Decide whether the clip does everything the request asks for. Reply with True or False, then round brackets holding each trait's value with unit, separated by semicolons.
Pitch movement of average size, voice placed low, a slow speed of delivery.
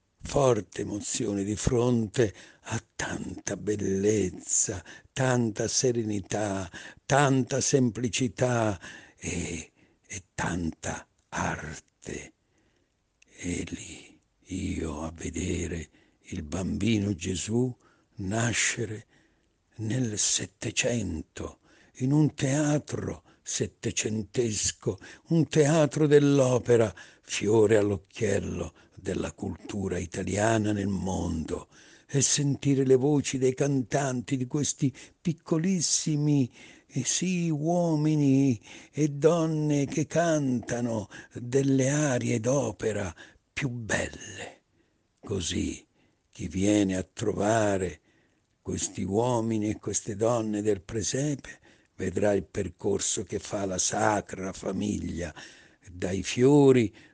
False (5.8 semitones; 115 Hz; 85 wpm)